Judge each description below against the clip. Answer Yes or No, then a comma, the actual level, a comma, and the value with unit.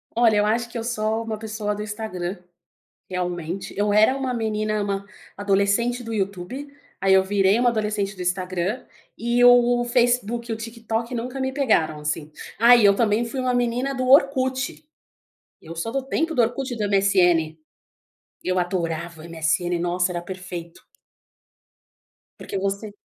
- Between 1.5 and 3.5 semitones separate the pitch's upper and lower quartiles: No, average, 4.5 semitones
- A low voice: No, high, 215 Hz